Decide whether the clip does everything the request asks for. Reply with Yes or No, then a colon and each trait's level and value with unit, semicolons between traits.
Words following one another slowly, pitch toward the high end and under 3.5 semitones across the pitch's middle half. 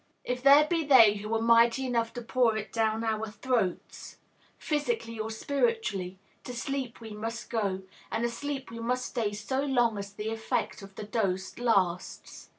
No: average, 170 wpm; high, 230 Hz; average, 3.1 semitones